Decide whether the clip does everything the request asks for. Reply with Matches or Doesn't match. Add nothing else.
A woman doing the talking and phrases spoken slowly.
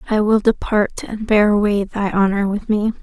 Doesn't match